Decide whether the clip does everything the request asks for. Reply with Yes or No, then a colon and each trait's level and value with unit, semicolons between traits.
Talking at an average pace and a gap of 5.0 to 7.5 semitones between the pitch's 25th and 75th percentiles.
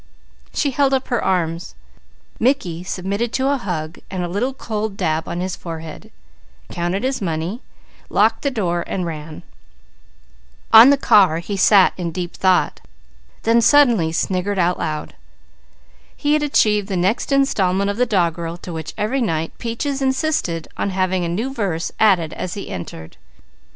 Yes: average, 155 wpm; wide, 5.6 semitones